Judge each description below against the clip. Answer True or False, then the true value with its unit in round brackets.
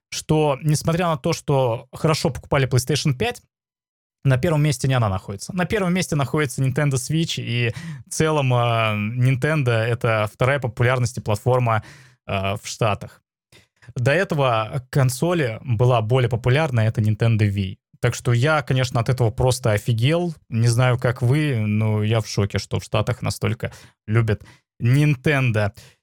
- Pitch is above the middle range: False (125 Hz)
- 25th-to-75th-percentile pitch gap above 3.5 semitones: True (4.7 semitones)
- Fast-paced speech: False (150 wpm)